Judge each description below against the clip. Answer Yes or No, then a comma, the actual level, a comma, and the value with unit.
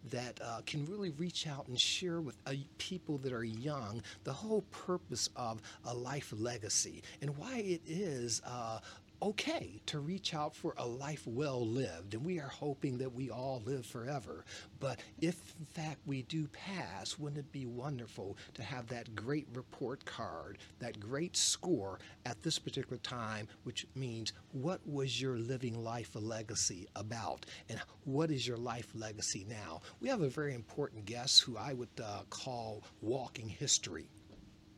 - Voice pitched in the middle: No, low, 125 Hz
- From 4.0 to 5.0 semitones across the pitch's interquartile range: Yes, average, 4.7 semitones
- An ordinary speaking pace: Yes, average, 170 wpm